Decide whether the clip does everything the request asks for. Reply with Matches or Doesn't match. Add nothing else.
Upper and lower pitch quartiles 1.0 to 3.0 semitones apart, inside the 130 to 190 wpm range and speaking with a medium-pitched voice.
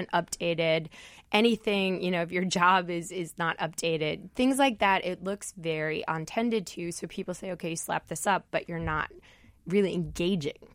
Matches